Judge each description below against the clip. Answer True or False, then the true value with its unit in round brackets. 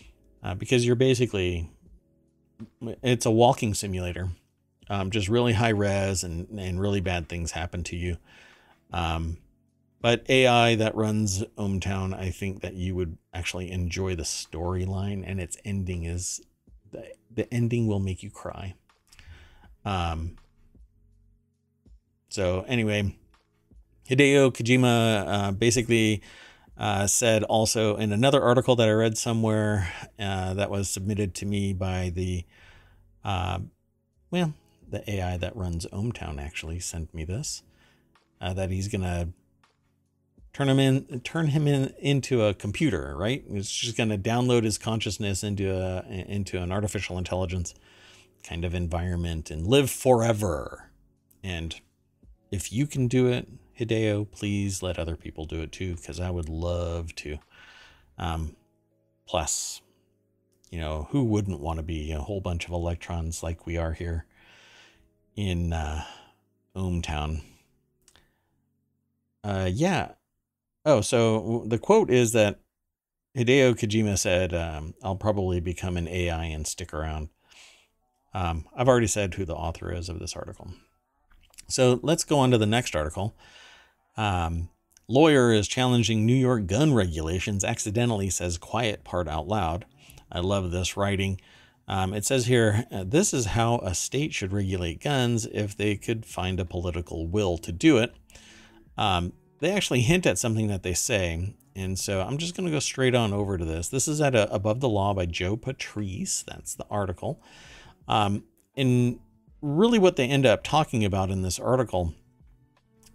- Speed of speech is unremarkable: True (150 wpm)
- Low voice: True (100 Hz)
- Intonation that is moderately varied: True (4.3 semitones)